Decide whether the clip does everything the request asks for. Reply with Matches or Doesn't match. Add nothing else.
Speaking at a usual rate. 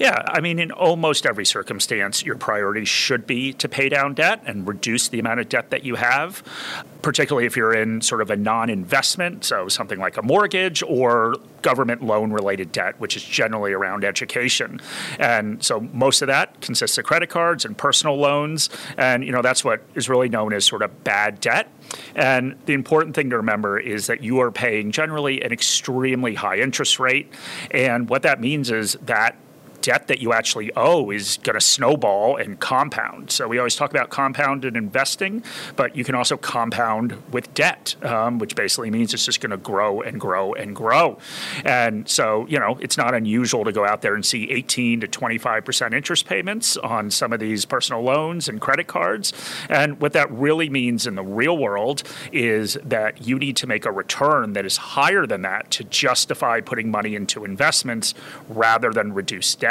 Matches